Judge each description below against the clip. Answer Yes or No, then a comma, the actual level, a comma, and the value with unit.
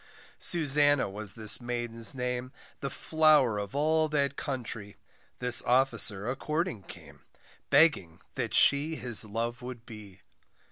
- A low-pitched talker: Yes, low, 125 Hz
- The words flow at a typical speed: No, slow, 130 wpm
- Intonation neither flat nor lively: Yes, average, 4.9 semitones